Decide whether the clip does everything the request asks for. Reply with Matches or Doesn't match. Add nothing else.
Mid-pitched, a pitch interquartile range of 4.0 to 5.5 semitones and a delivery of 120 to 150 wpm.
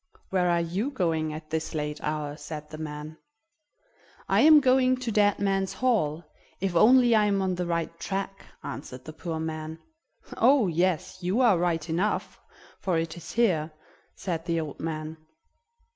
Doesn't match